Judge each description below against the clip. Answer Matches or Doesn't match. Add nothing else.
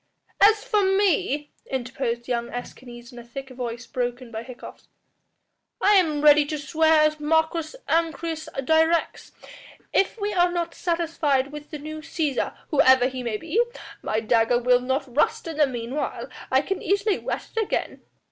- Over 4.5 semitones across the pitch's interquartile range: Matches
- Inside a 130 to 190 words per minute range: Matches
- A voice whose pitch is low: Doesn't match